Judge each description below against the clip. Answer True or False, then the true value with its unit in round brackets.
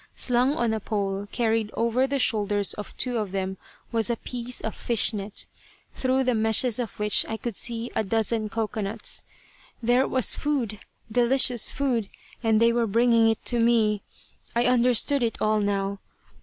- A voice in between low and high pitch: False (230 Hz)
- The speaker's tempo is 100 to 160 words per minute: False (170 wpm)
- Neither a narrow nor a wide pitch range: False (2.3 semitones)